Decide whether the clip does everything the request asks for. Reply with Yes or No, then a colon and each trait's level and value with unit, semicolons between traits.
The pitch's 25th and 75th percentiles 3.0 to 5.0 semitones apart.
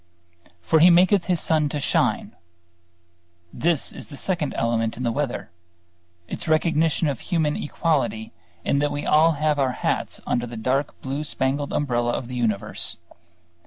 Yes: average, 4.3 semitones